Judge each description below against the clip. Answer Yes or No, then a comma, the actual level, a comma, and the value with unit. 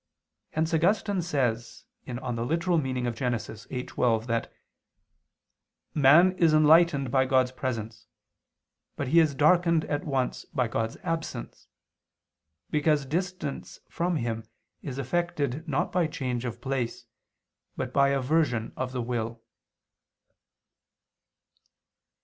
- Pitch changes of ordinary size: Yes, average, 4.7 semitones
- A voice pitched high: No, low, 135 Hz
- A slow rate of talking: Yes, slow, 110 wpm